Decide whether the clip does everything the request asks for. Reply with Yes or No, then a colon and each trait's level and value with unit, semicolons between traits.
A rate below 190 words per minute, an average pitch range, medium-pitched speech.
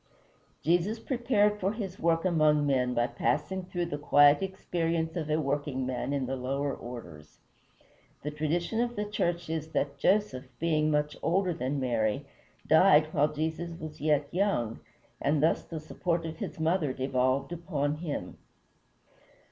Yes: average, 150 wpm; average, 3.6 semitones; medium, 155 Hz